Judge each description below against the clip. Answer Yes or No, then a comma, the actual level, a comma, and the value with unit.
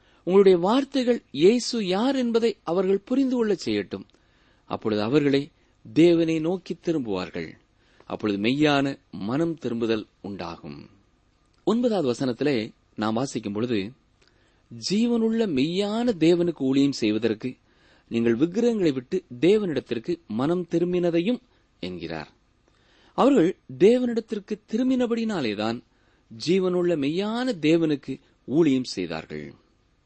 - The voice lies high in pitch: No, medium, 160 Hz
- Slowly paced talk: No, average, 90 wpm